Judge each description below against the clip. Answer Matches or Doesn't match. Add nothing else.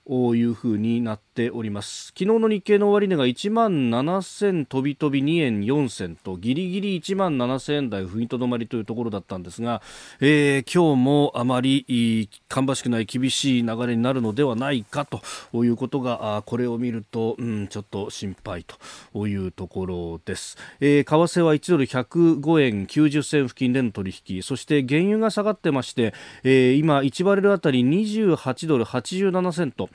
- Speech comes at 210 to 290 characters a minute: Doesn't match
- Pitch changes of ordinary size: Matches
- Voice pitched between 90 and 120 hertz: Doesn't match